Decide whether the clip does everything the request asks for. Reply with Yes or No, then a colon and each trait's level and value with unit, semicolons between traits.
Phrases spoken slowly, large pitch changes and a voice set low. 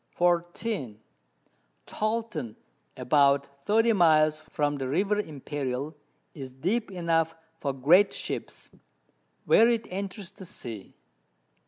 No: slow, 105 wpm; wide, 6.2 semitones; medium, 165 Hz